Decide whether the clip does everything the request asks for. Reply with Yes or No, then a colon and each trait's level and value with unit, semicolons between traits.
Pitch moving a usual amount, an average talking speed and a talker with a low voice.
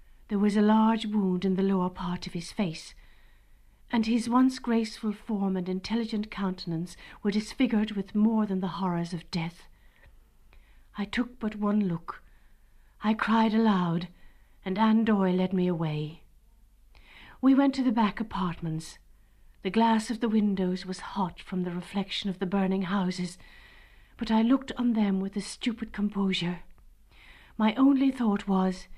No: average, 3.3 semitones; average, 155 wpm; high, 200 Hz